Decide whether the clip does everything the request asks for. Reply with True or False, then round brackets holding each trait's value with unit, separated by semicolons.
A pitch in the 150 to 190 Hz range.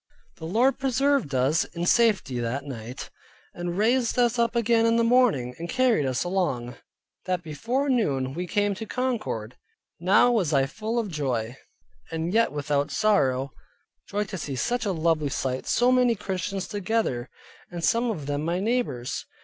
True (185 Hz)